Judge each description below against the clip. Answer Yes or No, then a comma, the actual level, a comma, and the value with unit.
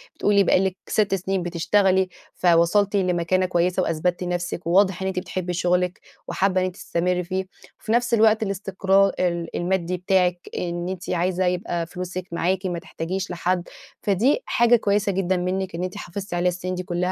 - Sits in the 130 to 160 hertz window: No, medium, 185 Hz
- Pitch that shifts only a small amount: Yes, narrow, 1.6 semitones